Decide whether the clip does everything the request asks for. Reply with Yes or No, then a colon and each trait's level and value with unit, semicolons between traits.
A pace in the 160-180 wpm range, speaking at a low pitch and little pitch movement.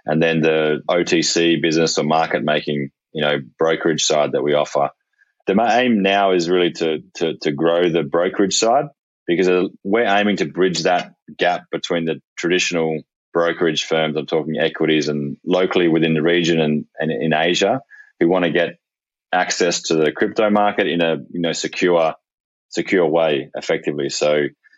Yes: average, 165 wpm; very low, 80 Hz; narrow, 2.2 semitones